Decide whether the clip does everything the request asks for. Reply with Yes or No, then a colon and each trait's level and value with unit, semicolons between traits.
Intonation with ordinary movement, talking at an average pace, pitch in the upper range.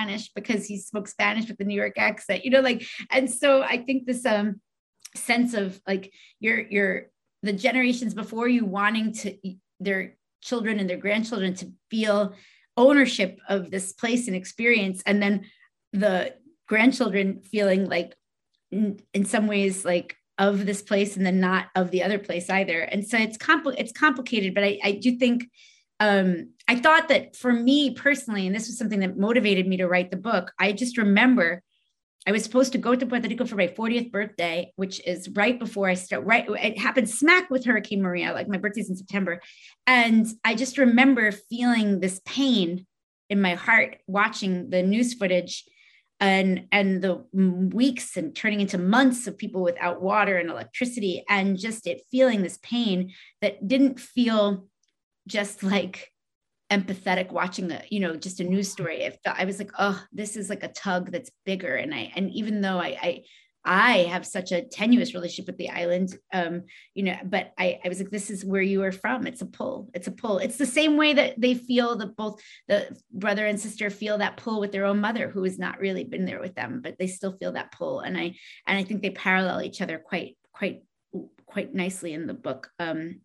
Yes: average, 3.8 semitones; average, 195 wpm; high, 205 Hz